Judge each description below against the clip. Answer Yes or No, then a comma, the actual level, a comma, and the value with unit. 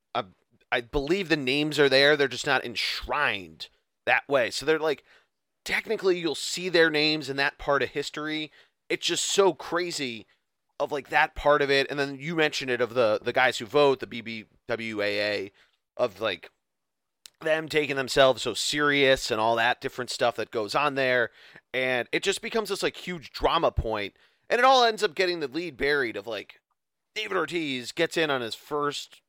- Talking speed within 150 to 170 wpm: No, average, 185 wpm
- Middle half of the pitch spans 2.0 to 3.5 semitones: No, average, 4.2 semitones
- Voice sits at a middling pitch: Yes, medium, 145 Hz